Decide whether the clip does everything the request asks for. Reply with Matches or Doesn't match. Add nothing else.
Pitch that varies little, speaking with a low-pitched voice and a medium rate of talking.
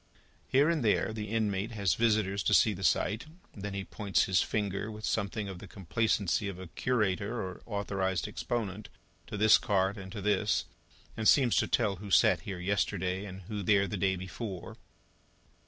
Matches